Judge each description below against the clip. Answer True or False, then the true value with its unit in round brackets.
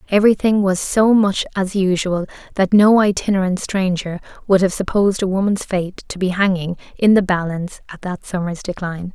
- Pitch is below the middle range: False (190 Hz)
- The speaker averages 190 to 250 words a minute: False (170 wpm)